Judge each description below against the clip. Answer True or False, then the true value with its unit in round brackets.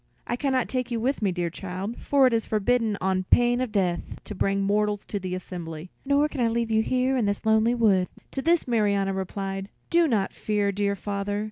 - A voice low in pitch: False (210 Hz)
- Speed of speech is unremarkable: False (220 wpm)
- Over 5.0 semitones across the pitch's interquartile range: False (3.9 semitones)